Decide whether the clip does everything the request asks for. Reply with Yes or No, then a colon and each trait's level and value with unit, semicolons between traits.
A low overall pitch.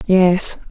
No: medium, 185 Hz